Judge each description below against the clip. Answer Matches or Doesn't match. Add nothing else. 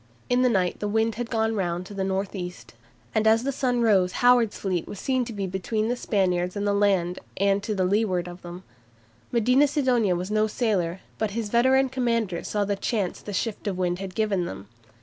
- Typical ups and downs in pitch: Matches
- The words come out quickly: Matches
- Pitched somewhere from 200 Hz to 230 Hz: Matches